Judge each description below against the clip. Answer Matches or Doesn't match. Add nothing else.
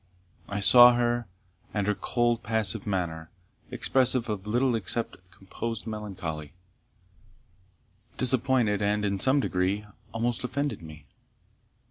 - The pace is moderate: Doesn't match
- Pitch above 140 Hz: Doesn't match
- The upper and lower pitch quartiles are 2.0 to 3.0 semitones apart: Doesn't match